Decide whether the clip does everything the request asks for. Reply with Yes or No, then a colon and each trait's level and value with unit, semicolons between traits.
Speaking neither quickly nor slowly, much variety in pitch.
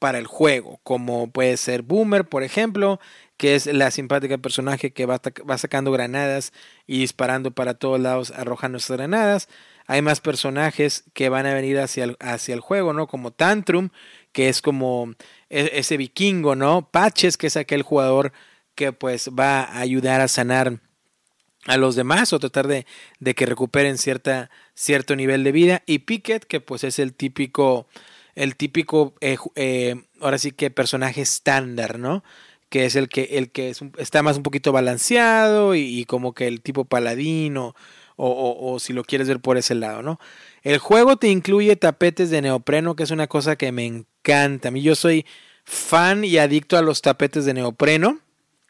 No: average, 180 wpm; average, 3.1 semitones